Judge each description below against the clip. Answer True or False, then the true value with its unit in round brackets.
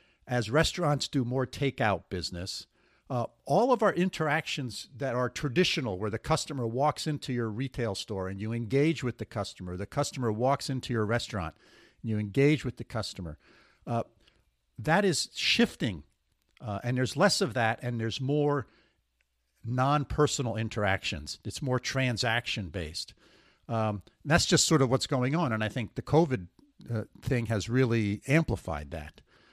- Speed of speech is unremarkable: True (160 wpm)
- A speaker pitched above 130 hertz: False (120 Hz)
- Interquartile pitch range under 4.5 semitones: False (5.0 semitones)